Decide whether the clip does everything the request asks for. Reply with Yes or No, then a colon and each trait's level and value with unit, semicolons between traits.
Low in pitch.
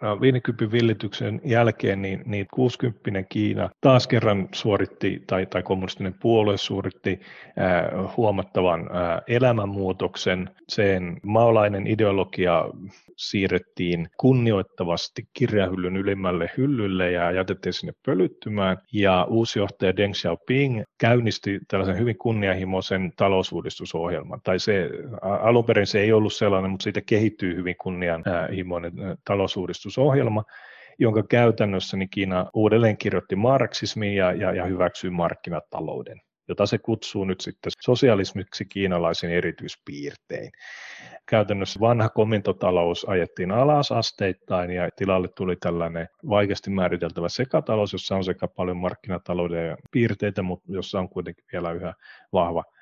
Yes: low, 100 Hz